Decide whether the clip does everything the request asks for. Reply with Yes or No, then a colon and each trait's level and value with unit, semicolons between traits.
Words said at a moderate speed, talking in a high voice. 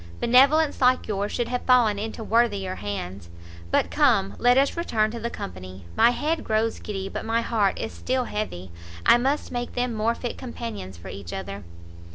Yes: average, 185 wpm; high, 225 Hz